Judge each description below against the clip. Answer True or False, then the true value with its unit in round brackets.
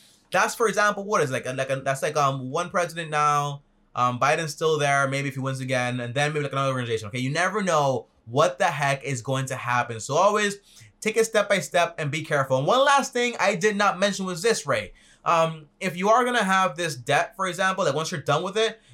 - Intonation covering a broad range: True (6.3 semitones)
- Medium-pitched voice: True (155 Hz)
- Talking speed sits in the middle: False (255 wpm)